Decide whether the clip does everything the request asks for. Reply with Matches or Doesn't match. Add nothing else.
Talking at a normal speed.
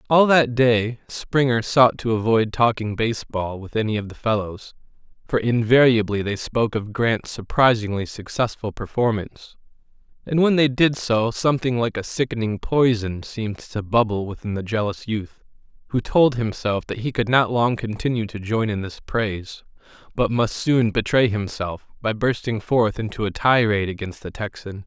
Matches